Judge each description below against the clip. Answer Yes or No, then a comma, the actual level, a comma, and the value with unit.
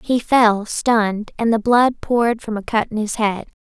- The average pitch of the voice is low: No, high, 225 Hz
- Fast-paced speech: Yes, fast, 215 wpm